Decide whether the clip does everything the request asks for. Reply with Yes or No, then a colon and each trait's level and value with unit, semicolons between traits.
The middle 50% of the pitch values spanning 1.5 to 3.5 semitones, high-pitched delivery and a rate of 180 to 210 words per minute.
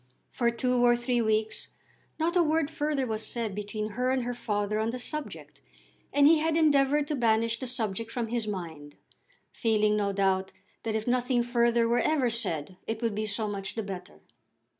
Yes: average, 3.1 semitones; high, 230 Hz; average, 190 wpm